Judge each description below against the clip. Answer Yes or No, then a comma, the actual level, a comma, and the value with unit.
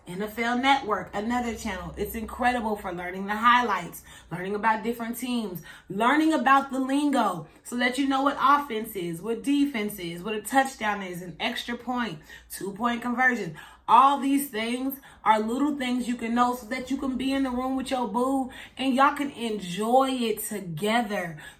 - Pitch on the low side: No, high, 240 Hz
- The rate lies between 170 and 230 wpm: Yes, average, 180 wpm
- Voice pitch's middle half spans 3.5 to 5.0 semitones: Yes, average, 4.0 semitones